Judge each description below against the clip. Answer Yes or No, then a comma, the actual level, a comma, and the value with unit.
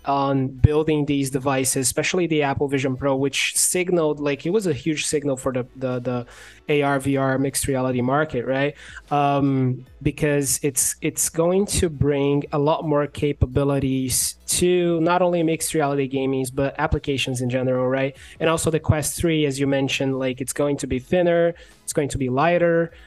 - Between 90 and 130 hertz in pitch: No, medium, 140 Hz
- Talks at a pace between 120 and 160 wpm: No, average, 175 wpm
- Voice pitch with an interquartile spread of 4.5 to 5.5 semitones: No, average, 2.7 semitones